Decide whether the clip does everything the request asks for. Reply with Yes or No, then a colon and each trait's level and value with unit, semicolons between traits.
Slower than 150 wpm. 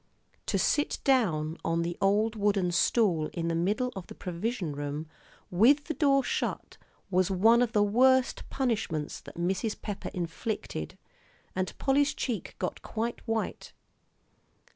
Yes: average, 140 wpm